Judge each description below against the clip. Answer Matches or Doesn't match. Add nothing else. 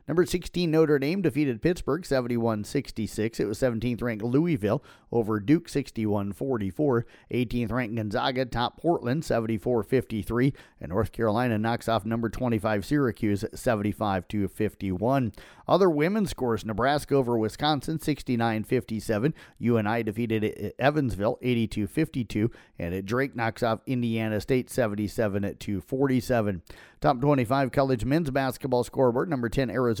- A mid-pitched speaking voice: Doesn't match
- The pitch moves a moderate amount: Matches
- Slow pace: Matches